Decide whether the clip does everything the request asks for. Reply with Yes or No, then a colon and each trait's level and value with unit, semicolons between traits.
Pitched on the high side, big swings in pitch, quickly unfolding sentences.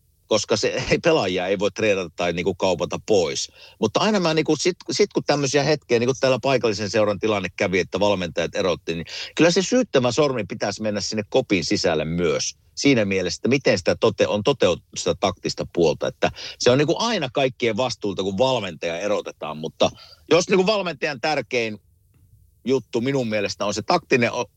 No: low, 125 Hz; wide, 6.7 semitones; fast, 180 wpm